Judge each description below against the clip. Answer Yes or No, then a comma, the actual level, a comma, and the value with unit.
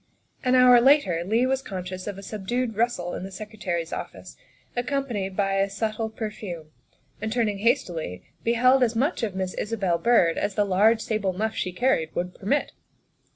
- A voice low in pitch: No, high, 215 Hz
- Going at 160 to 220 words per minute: Yes, average, 175 wpm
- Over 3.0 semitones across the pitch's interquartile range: Yes, average, 4.2 semitones